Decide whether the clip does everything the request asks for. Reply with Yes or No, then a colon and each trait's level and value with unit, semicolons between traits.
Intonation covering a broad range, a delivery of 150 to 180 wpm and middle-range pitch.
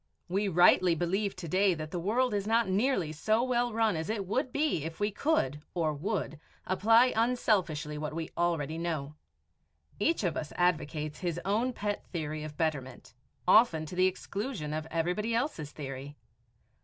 Yes: wide, 5.7 semitones; average, 170 wpm; medium, 180 Hz